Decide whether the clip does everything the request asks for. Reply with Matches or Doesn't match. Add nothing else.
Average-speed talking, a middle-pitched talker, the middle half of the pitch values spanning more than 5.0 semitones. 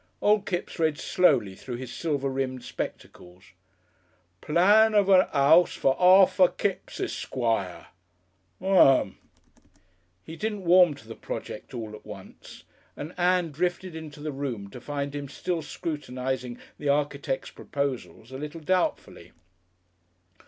Doesn't match